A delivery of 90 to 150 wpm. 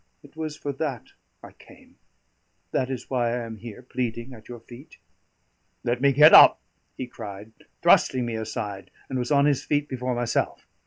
No: average, 175 wpm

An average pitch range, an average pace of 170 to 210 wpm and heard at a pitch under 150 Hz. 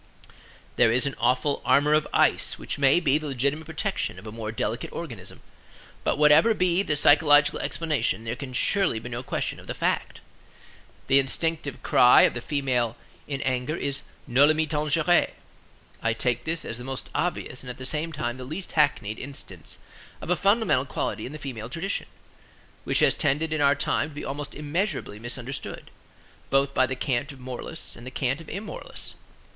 Yes: average, 3.7 semitones; average, 185 wpm; medium, 140 Hz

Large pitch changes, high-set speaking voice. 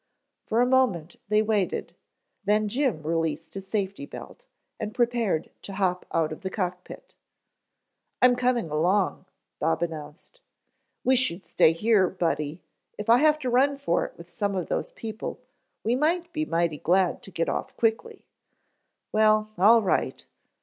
Yes: wide, 5.9 semitones; high, 205 Hz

